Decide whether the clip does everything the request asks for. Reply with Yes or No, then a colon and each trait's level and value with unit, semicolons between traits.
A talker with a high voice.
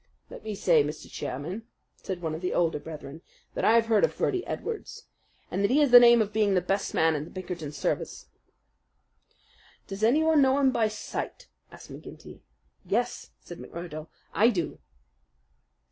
Yes: high, 195 Hz